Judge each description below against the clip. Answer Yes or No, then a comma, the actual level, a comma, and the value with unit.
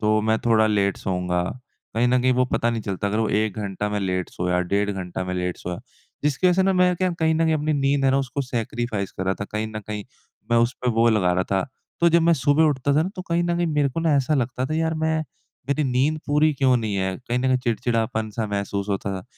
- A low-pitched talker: Yes, low, 120 Hz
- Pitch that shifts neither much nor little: No, wide, 6.5 semitones